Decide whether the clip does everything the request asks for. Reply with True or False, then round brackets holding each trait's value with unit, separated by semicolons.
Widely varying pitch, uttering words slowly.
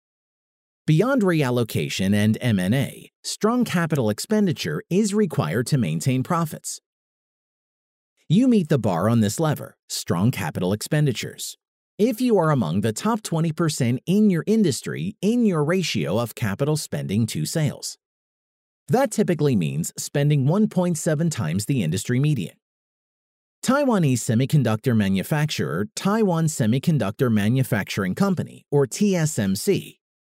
True (7.8 semitones; 115 wpm)